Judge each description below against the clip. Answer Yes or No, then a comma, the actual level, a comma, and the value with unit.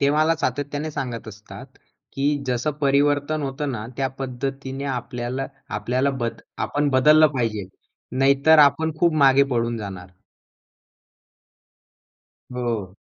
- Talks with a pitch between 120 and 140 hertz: Yes, low, 135 Hz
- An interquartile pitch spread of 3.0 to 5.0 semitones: Yes, average, 3.3 semitones